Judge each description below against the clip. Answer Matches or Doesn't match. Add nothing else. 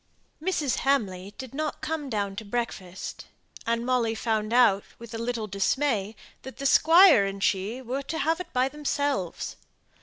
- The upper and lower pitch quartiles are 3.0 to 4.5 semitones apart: Doesn't match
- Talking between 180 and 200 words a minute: Doesn't match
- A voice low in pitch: Doesn't match